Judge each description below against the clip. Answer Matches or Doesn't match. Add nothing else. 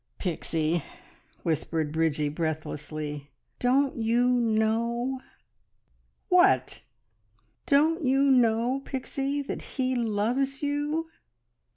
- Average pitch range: Doesn't match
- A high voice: Matches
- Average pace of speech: Doesn't match